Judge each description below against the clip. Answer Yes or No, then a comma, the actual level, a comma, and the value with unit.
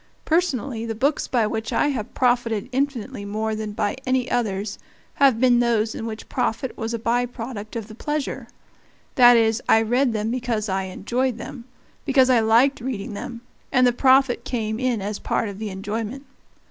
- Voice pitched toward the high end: Yes, high, 235 Hz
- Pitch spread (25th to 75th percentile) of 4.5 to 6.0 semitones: No, average, 2.9 semitones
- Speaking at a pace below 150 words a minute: No, average, 185 wpm